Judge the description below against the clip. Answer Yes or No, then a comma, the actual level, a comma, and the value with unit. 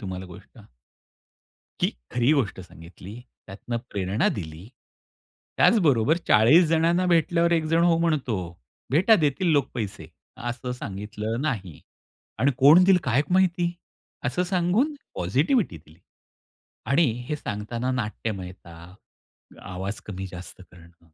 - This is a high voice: No, low, 120 Hz